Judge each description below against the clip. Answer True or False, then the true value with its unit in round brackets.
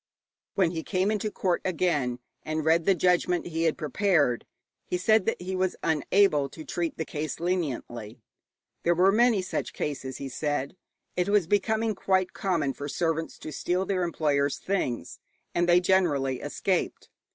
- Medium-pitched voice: True (175 Hz)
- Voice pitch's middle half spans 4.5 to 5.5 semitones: False (4.1 semitones)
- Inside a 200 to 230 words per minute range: False (165 wpm)